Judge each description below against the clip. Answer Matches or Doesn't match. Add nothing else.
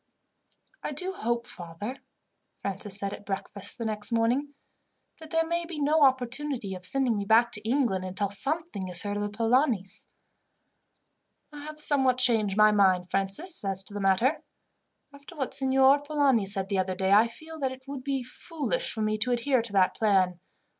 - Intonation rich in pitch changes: Matches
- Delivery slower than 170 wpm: Doesn't match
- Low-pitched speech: Doesn't match